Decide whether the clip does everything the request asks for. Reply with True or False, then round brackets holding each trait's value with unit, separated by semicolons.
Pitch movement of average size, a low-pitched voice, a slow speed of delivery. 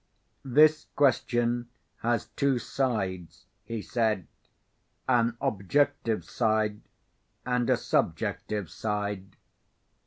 True (3.0 semitones; 115 Hz; 85 wpm)